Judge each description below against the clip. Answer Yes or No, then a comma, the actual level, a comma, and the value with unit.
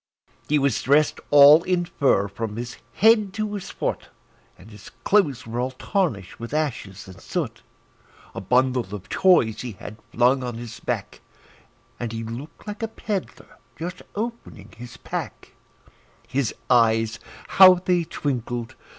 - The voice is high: No, low, 130 Hz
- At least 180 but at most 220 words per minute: No, average, 150 wpm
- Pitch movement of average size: No, wide, 7.6 semitones